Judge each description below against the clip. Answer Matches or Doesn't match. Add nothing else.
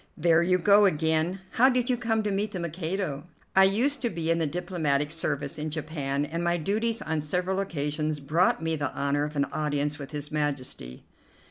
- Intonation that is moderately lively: Matches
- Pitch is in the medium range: Matches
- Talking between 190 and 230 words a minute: Matches